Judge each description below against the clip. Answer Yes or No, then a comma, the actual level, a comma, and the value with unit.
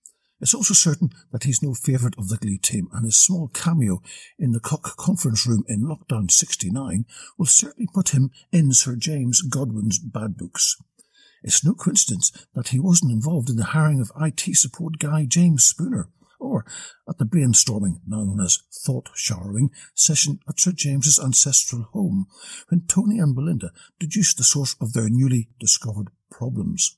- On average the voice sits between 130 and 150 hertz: Yes, medium, 140 Hz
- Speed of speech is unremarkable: Yes, average, 170 wpm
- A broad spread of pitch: Yes, wide, 6.4 semitones